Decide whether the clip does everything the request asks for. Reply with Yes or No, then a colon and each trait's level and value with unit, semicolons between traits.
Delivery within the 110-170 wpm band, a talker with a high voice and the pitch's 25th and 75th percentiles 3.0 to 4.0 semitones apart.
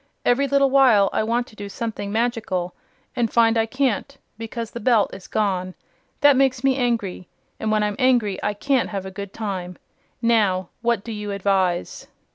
No: average, 180 wpm; high, 220 Hz; average, 3.5 semitones